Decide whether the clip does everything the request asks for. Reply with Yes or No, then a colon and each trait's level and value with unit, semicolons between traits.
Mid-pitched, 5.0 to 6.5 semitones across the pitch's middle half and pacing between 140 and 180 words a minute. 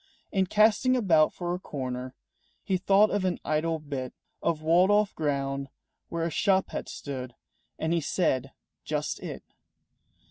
Yes: medium, 165 Hz; average, 5.3 semitones; average, 150 wpm